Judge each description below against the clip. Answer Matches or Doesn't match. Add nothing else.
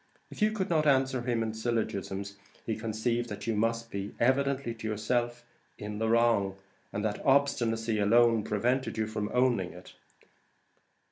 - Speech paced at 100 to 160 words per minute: Matches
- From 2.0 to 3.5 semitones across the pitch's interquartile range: Matches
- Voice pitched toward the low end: Matches